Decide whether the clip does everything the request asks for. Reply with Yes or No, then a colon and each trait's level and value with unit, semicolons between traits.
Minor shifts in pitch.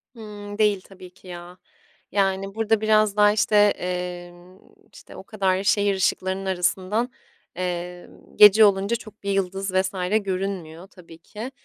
Yes: narrow, 2.3 semitones